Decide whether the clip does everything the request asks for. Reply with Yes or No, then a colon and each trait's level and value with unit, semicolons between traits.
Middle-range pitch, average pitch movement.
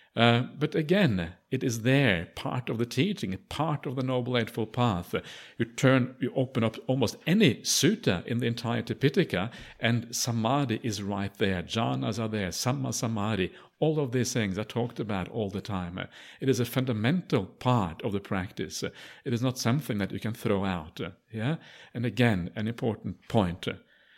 No: low, 120 Hz; average, 3.4 semitones